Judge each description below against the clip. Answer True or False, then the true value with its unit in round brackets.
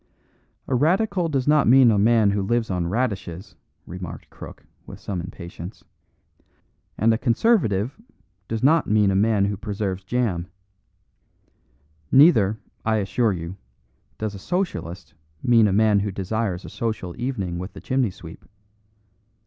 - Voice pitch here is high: False (105 Hz)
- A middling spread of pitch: True (4.3 semitones)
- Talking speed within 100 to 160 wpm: True (140 wpm)